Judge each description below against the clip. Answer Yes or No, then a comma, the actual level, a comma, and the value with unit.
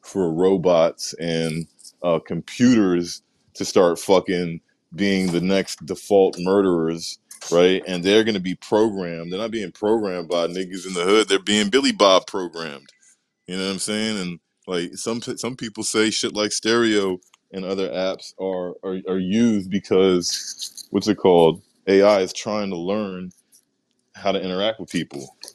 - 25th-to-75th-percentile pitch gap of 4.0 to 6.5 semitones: No, narrow, 2.6 semitones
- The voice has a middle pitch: No, very low, 95 Hz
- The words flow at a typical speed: Yes, average, 160 wpm